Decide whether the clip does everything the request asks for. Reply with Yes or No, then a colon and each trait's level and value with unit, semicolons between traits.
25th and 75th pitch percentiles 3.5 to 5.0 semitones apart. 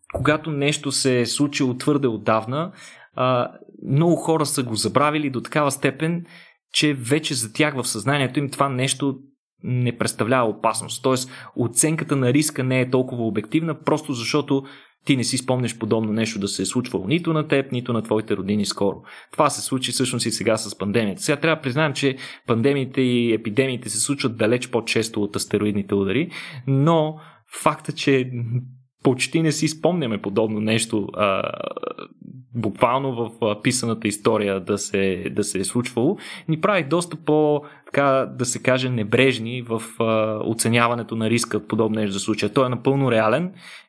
Yes: average, 4.5 semitones